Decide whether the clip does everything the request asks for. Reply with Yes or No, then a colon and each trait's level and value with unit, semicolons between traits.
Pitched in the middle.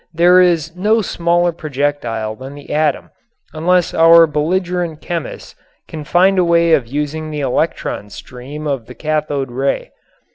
Yes: medium, 155 Hz